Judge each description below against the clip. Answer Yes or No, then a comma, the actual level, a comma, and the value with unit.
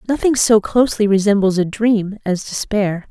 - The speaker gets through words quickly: No, average, 155 wpm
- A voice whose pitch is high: Yes, high, 210 Hz